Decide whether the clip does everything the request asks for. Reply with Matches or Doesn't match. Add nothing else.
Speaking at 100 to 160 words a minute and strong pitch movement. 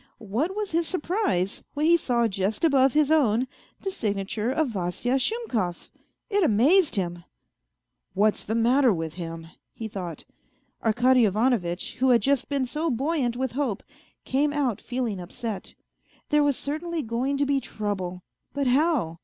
Doesn't match